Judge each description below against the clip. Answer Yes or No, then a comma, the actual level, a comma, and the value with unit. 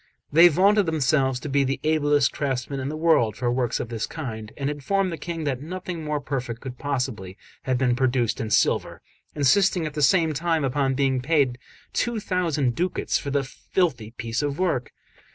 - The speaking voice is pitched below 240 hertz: Yes, medium, 140 Hz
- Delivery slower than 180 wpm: No, average, 190 wpm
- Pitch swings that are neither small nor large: Yes, average, 4.2 semitones